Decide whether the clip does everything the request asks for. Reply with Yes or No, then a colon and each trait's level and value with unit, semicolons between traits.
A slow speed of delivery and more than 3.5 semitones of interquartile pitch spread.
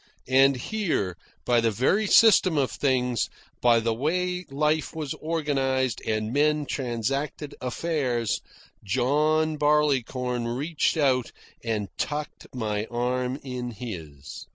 Yes: slow, 115 wpm; average, 4.2 semitones